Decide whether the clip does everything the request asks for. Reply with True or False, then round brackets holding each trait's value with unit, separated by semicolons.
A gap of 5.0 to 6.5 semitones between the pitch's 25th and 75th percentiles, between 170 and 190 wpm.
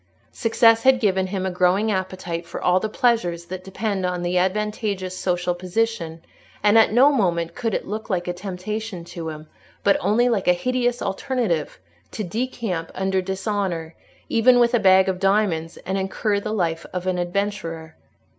False (3.5 semitones; 175 wpm)